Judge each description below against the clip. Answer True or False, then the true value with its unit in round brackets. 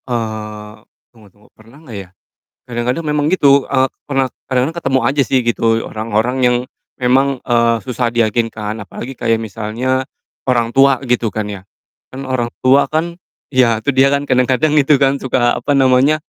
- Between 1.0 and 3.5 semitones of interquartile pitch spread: True (3.0 semitones)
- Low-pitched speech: True (125 Hz)